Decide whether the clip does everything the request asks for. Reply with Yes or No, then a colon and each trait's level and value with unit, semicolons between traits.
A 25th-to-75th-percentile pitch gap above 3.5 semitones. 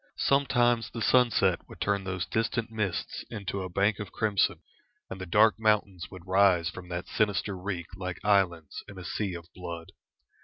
No: average, 3.0 semitones